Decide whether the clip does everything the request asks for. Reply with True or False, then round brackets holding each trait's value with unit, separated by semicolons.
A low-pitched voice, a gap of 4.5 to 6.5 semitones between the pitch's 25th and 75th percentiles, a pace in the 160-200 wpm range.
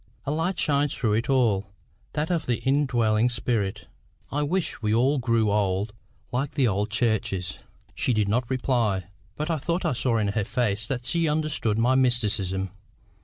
True (120 Hz; 4.8 semitones; 170 wpm)